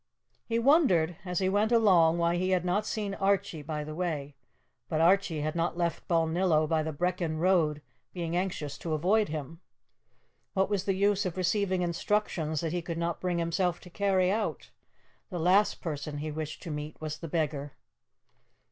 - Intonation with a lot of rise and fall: No, average, 3.3 semitones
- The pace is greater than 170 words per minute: Yes, average, 180 wpm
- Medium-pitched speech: Yes, medium, 175 Hz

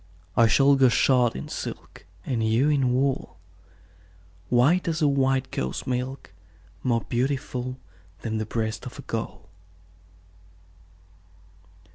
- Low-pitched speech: Yes, low, 130 Hz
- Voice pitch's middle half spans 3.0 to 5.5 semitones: No, narrow, 2.6 semitones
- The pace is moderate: No, slow, 120 wpm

